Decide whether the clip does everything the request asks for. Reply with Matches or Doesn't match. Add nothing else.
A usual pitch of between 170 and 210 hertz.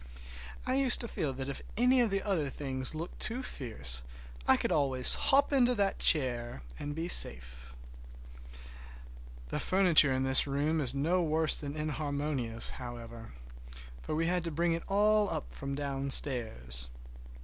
Doesn't match